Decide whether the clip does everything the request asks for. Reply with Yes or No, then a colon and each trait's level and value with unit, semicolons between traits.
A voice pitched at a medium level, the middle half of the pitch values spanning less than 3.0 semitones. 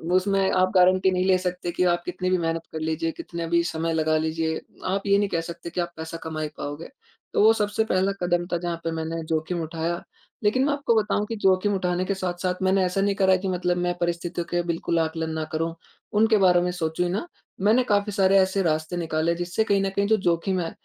Yes: medium, 180 Hz; narrow, 2.6 semitones